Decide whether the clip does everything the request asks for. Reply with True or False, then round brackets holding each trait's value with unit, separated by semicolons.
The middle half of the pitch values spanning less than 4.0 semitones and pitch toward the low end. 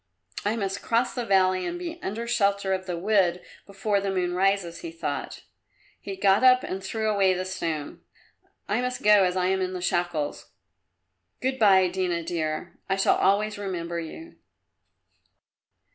False (2.8 semitones; 195 Hz)